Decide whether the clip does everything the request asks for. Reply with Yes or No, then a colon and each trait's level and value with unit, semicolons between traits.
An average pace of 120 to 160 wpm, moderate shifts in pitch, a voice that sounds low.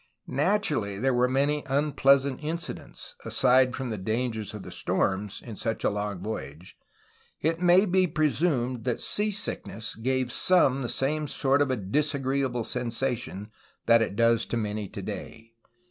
Yes: average, 155 wpm; average, 4.6 semitones; low, 130 Hz